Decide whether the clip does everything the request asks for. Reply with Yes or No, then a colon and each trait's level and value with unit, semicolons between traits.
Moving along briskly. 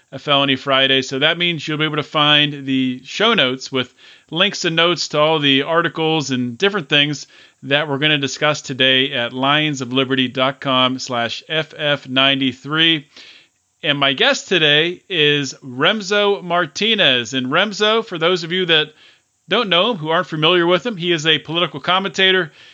No: average, 160 wpm